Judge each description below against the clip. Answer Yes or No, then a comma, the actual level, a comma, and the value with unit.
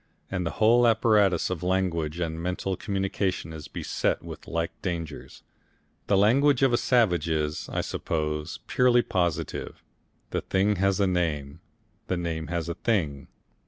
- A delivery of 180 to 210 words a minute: No, average, 150 wpm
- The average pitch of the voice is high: No, very low, 90 Hz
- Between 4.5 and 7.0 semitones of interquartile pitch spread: No, average, 3.9 semitones